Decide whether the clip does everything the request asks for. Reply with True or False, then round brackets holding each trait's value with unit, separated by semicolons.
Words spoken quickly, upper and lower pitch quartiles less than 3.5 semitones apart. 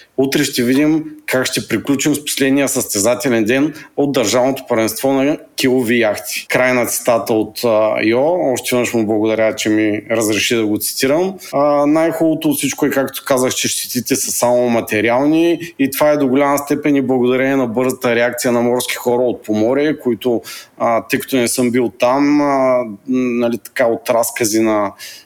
True (170 wpm; 3.0 semitones)